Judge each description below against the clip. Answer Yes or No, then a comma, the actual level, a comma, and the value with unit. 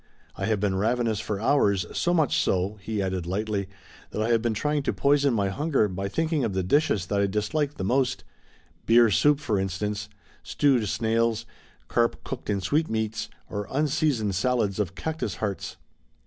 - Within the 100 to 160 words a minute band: No, average, 175 wpm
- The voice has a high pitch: No, low, 110 Hz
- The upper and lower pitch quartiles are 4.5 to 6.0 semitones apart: Yes, average, 5.3 semitones